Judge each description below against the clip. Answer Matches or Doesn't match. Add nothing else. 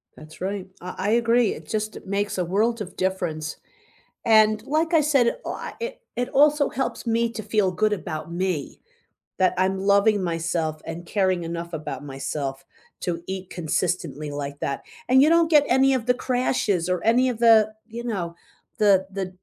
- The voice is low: Doesn't match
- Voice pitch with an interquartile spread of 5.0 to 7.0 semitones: Matches